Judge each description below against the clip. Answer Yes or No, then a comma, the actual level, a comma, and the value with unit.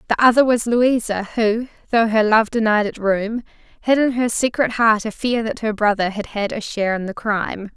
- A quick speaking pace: Yes, fast, 215 wpm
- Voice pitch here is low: No, high, 220 Hz